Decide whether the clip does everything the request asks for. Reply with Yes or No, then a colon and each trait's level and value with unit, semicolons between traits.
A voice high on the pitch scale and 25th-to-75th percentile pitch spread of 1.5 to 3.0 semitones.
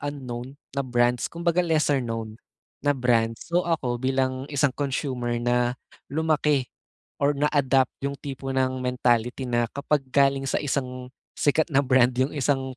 No: low, 135 Hz; narrow, 2.5 semitones